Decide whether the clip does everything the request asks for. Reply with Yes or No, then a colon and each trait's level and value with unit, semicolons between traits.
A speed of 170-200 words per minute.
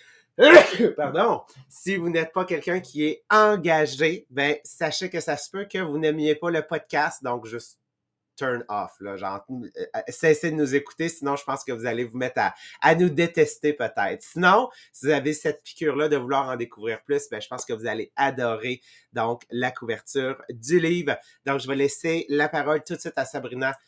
Yes: average, 195 wpm